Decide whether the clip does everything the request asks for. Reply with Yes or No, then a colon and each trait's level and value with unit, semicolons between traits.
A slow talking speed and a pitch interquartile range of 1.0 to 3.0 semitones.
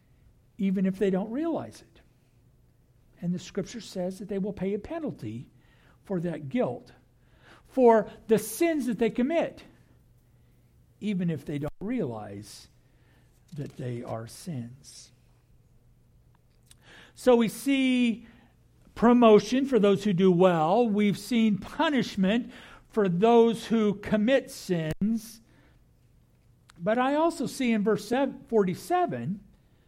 No: slow, 115 wpm; average, 5.2 semitones